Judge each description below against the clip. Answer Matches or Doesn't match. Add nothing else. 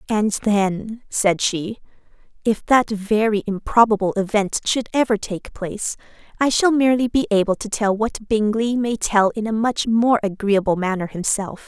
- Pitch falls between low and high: Doesn't match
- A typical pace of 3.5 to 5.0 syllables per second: Matches